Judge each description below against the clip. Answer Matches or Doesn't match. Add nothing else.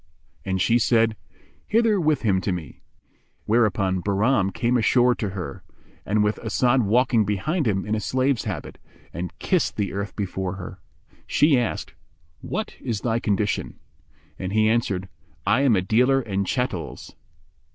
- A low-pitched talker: Matches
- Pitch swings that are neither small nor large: Matches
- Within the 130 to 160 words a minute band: Matches